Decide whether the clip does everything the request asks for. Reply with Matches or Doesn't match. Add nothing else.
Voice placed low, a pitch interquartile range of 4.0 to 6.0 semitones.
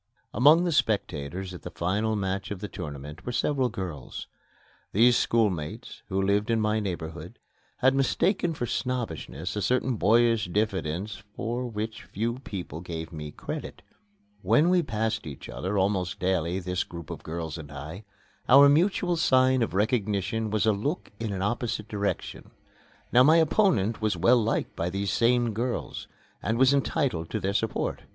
Matches